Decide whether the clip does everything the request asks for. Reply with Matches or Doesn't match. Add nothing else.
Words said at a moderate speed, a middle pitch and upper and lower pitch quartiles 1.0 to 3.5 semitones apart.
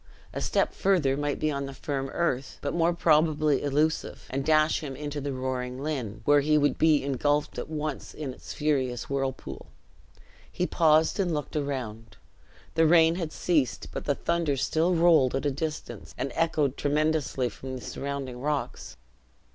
Matches